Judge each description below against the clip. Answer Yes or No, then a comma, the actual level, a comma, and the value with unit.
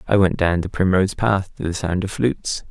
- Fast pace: Yes, fast, 245 wpm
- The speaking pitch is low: Yes, very low, 95 Hz